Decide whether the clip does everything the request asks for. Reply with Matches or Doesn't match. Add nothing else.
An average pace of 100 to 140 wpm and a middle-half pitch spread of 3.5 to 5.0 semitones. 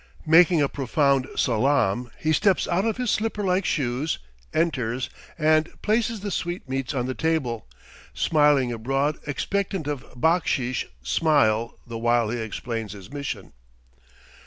Doesn't match